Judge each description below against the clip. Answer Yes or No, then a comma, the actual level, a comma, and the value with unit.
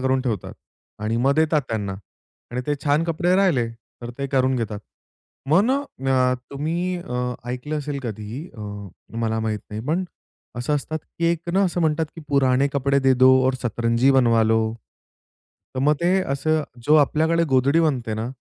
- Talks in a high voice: No, low, 135 Hz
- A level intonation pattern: No, average, 5.0 semitones